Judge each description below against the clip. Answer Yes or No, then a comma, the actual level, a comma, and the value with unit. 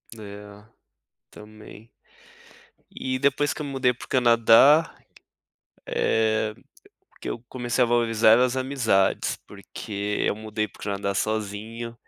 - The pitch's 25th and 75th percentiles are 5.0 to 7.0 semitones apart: No, average, 3.0 semitones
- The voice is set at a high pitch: No, low, 115 Hz